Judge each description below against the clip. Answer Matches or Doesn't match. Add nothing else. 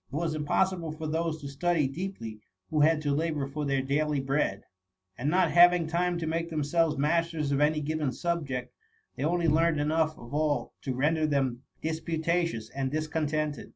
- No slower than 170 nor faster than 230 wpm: Matches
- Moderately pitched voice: Matches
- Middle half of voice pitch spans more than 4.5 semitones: Doesn't match